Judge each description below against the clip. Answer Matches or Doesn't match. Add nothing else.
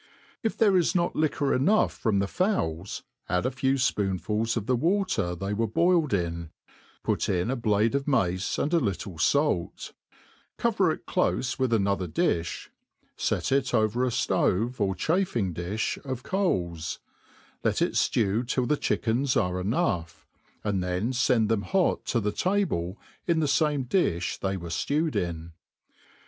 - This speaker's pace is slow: Doesn't match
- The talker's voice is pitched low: Matches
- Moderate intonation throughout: Doesn't match